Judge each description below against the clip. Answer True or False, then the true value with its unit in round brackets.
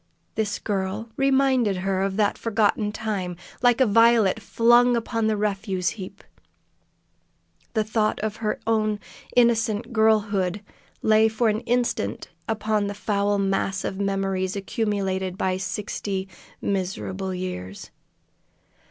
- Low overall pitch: False (210 Hz)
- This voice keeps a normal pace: False (120 wpm)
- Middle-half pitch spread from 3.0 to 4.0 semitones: False (2.5 semitones)